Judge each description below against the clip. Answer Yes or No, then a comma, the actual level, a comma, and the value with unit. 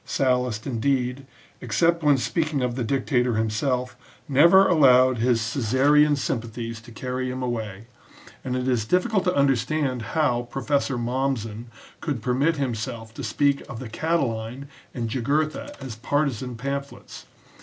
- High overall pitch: No, low, 130 Hz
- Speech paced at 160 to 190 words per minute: No, average, 150 wpm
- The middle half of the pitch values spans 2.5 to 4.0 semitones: Yes, average, 3.1 semitones